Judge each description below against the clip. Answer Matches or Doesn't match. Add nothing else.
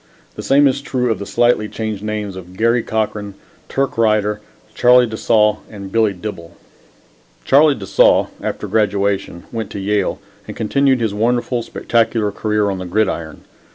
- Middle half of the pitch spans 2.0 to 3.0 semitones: Matches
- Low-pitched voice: Matches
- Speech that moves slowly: Doesn't match